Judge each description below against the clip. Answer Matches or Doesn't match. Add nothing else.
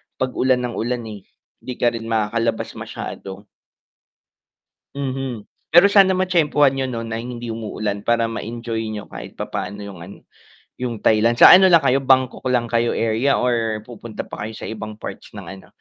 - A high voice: Doesn't match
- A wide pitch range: Doesn't match